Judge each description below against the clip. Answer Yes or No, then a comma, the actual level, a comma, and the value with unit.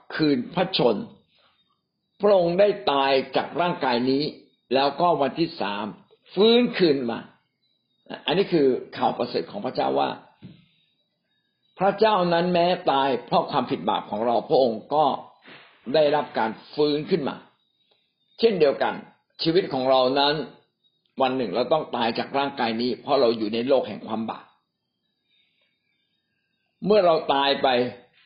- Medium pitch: Yes, medium, 160 Hz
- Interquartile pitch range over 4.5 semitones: Yes, wide, 5.6 semitones